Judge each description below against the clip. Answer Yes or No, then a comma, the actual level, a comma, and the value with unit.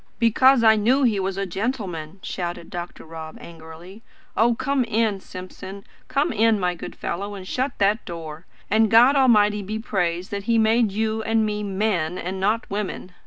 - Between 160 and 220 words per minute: Yes, average, 175 wpm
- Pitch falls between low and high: No, high, 205 Hz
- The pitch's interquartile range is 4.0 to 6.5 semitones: No, average, 3.5 semitones